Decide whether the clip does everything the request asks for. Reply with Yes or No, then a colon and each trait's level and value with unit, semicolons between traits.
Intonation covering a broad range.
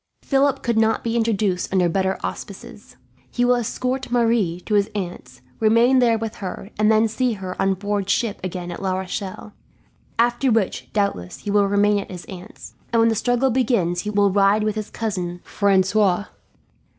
No: average, 3.3 semitones